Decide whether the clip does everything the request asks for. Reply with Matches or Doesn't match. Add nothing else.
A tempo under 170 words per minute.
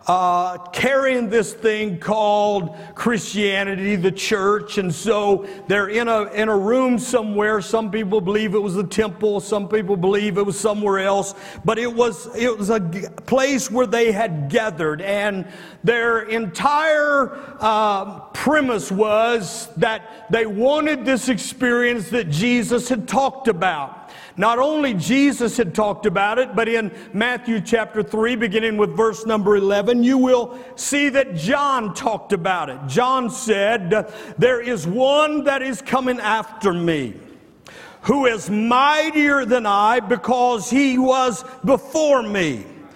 Matches